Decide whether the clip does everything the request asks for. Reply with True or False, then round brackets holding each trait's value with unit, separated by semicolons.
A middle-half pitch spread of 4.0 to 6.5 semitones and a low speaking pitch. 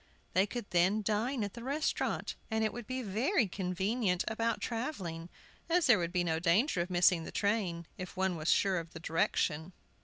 False (4.7 semitones; 195 Hz)